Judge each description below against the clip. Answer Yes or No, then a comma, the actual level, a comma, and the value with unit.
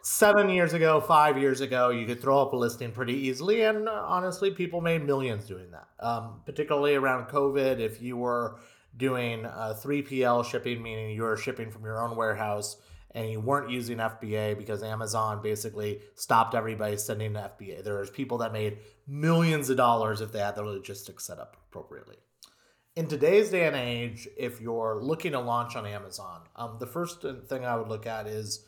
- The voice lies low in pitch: Yes, low, 120 Hz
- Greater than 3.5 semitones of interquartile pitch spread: Yes, average, 4.2 semitones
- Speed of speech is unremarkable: Yes, average, 185 wpm